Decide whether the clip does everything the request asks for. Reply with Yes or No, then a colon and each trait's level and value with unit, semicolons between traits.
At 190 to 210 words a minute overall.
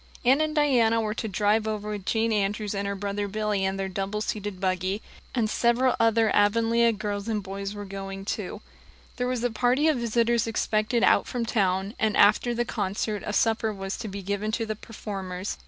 Yes: average, 200 wpm